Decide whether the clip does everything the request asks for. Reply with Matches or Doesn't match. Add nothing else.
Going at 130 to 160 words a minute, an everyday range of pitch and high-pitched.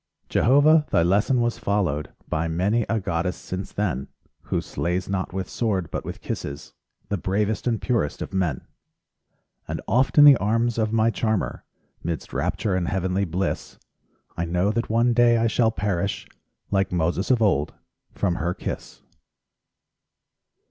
Doesn't match